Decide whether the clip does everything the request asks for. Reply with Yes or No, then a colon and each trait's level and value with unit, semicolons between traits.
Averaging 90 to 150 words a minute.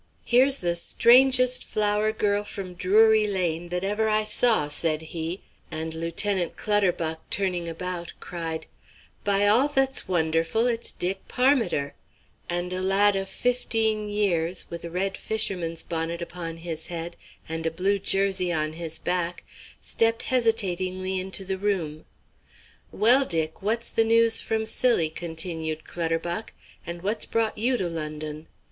Yes: average, 140 wpm